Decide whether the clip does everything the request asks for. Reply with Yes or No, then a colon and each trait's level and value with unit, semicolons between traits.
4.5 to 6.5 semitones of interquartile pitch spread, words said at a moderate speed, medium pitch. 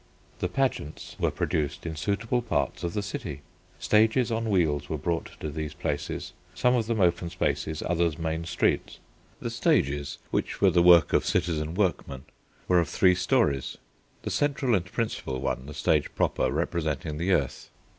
No: average, 5.2 semitones; average, 165 wpm; very low, 85 Hz